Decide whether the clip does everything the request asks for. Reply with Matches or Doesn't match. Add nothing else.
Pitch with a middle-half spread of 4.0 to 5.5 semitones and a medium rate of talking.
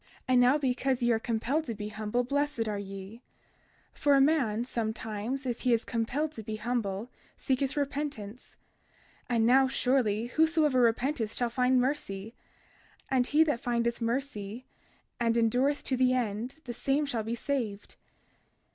Doesn't match